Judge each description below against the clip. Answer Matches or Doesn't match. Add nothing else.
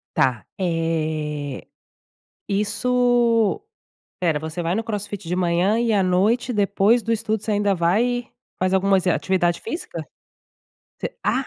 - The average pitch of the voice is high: Matches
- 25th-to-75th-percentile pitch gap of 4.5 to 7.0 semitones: Matches